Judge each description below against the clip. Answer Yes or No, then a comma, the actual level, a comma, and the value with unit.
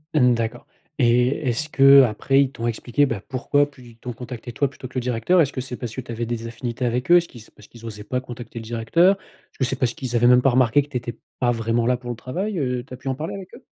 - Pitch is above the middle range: No, low, 125 Hz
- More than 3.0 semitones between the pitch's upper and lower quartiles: No, narrow, 2.5 semitones